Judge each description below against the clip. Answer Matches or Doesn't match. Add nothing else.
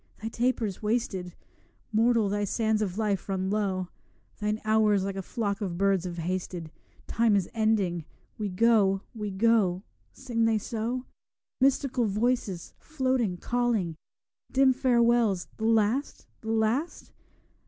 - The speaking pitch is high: Matches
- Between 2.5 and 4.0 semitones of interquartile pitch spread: Matches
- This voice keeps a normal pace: Doesn't match